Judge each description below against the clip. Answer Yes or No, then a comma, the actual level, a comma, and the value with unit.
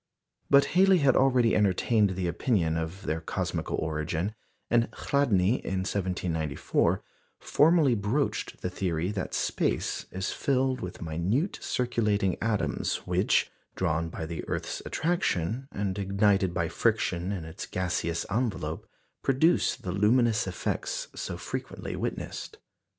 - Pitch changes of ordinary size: No, wide, 6.2 semitones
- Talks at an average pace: No, slow, 125 wpm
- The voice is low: Yes, low, 100 Hz